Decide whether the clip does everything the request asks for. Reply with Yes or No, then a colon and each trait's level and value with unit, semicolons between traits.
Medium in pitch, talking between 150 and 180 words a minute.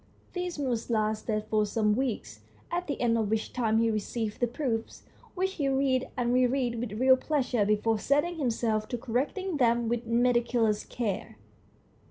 No: high, 240 Hz; average, 170 wpm